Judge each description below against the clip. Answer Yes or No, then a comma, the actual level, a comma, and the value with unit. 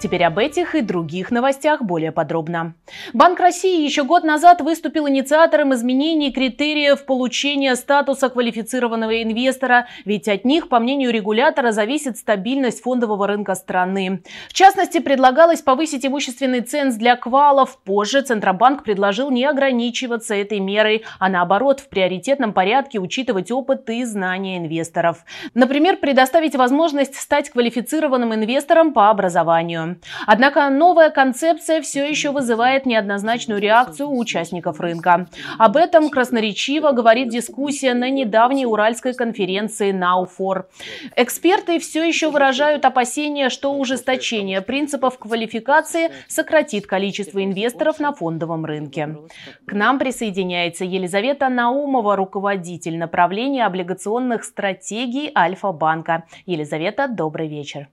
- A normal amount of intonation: No, wide, 6.2 semitones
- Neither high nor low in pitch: No, high, 245 Hz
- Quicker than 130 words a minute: No, average, 120 wpm